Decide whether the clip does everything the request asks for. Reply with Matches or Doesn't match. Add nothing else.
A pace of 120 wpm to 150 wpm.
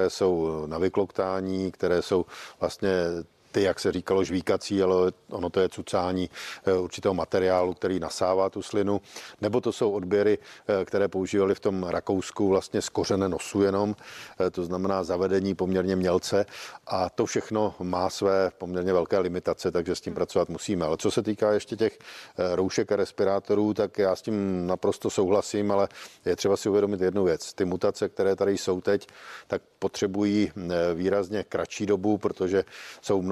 Doesn't match